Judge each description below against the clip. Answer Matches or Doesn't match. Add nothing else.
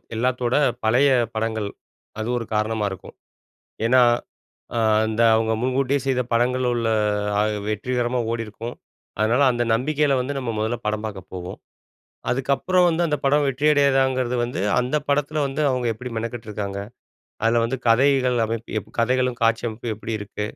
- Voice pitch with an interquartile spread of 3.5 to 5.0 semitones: Doesn't match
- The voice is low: Matches